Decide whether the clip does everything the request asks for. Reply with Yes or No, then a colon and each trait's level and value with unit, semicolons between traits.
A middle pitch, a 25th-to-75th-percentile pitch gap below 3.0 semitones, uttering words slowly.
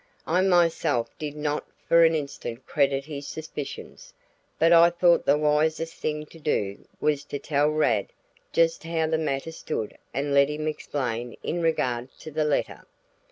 No: medium, 150 Hz; narrow, 2.6 semitones; average, 160 wpm